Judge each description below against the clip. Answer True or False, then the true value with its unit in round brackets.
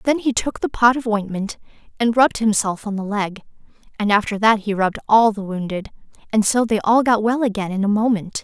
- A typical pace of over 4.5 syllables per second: True (5.7 syllables/s)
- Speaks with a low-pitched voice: False (215 Hz)